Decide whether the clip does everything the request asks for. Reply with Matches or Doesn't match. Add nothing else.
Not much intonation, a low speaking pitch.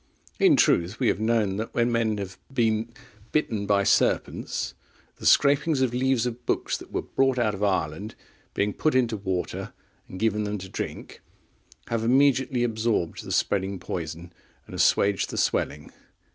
Doesn't match